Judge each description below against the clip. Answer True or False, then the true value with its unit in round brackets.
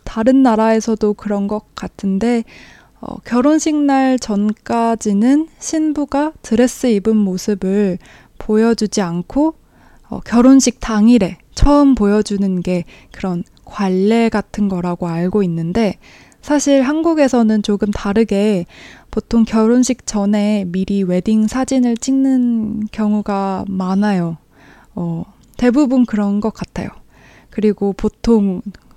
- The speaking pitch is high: True (215 Hz)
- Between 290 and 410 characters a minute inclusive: False (240 characters per minute)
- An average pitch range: True (3.5 semitones)